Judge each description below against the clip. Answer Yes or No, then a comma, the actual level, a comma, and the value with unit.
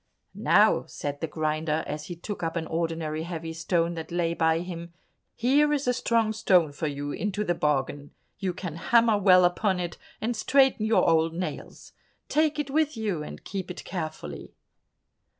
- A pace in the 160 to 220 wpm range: Yes, average, 175 wpm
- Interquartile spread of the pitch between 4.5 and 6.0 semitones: Yes, average, 5.0 semitones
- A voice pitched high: No, medium, 175 Hz